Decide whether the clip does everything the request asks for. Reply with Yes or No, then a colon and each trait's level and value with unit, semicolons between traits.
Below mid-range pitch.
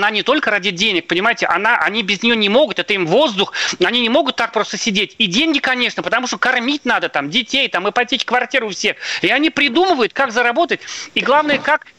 No: high, 245 Hz